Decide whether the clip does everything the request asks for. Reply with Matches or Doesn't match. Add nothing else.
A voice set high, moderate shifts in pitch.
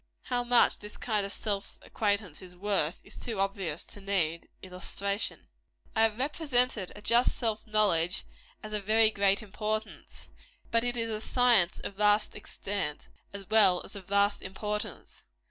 Doesn't match